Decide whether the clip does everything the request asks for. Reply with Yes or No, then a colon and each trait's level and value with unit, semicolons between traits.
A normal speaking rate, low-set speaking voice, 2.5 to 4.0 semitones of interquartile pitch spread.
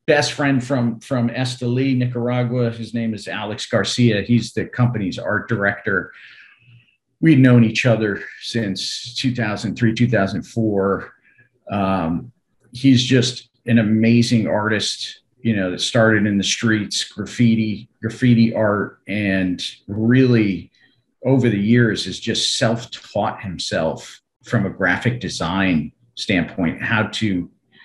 No: slow, 120 wpm; low, 115 Hz; average, 2.8 semitones